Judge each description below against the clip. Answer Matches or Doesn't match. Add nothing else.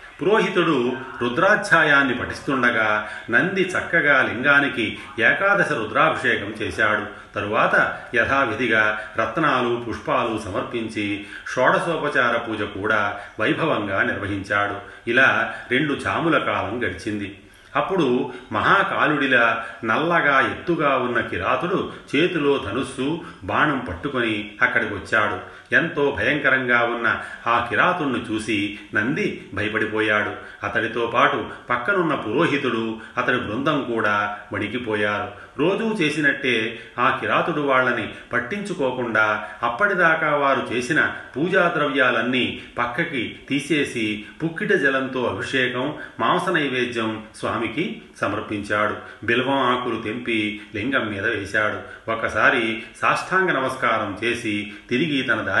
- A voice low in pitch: Matches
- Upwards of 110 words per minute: Doesn't match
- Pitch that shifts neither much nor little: Matches